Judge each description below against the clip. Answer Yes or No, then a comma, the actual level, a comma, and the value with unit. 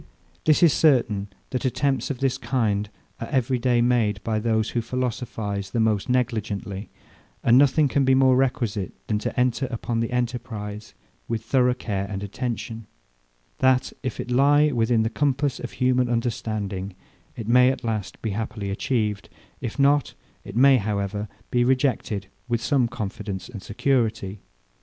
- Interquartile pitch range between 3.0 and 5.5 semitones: Yes, average, 3.4 semitones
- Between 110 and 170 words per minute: Yes, average, 160 wpm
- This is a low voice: Yes, low, 120 Hz